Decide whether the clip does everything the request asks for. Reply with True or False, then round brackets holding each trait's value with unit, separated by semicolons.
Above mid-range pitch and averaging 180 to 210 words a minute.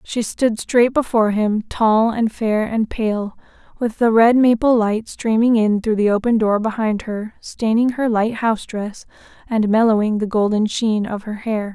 True (220 Hz; 185 wpm)